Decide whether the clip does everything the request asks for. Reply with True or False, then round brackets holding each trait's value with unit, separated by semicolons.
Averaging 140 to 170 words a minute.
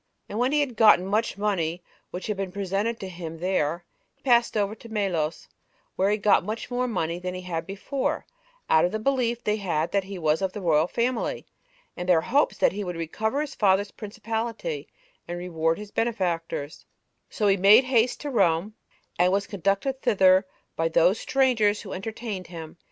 False (190 wpm)